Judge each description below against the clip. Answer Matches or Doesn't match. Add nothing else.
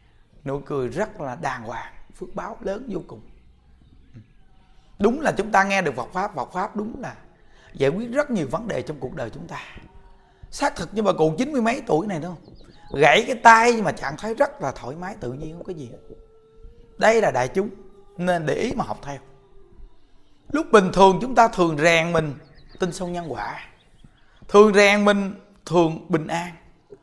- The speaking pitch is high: Doesn't match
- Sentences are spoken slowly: Doesn't match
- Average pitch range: Doesn't match